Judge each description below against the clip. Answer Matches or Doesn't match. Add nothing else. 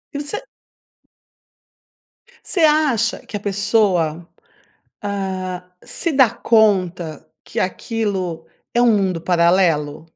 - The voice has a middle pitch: Doesn't match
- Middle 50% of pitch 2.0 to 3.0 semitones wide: Doesn't match